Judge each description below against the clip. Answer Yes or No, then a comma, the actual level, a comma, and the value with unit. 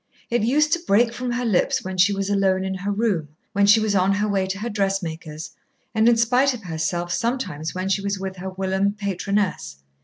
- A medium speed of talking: No, fast, 215 wpm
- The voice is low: No, high, 195 Hz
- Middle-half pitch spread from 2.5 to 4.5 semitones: Yes, average, 2.8 semitones